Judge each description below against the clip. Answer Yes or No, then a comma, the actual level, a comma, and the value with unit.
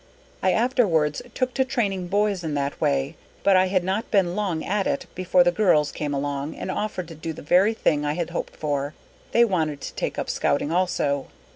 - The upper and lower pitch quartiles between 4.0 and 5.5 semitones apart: Yes, average, 5.2 semitones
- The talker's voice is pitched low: No, medium, 180 Hz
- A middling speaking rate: No, fast, 215 wpm